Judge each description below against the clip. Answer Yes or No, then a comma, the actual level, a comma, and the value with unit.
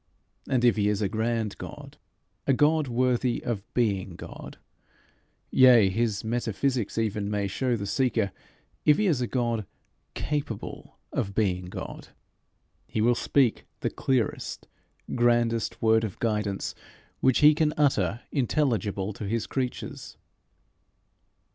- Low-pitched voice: Yes, low, 115 Hz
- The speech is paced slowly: Yes, slow, 130 wpm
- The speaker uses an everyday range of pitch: Yes, average, 3.6 semitones